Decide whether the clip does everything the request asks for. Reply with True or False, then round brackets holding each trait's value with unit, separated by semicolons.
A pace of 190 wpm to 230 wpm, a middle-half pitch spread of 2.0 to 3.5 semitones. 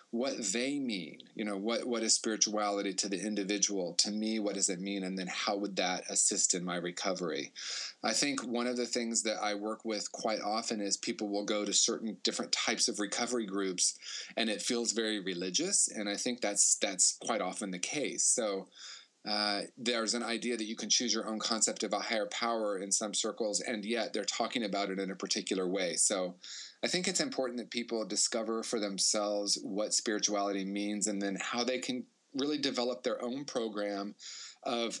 True (200 wpm; 2.7 semitones)